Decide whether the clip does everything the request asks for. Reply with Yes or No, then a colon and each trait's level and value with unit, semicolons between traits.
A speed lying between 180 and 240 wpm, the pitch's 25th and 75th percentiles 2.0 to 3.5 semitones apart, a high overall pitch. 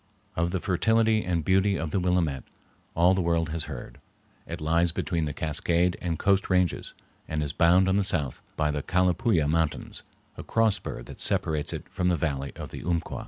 No: average, 195 wpm; average, 2.9 semitones; very low, 85 Hz